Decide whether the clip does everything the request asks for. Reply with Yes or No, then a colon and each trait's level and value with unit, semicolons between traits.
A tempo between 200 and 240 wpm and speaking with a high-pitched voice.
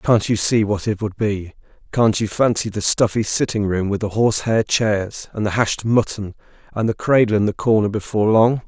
No: fast, 205 wpm; low, 105 Hz